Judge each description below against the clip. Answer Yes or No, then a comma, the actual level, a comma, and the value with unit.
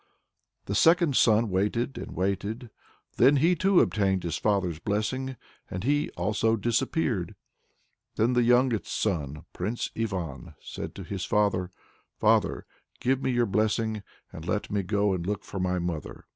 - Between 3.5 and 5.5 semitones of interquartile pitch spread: Yes, average, 4.6 semitones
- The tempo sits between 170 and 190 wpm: No, average, 150 wpm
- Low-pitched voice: Yes, low, 105 Hz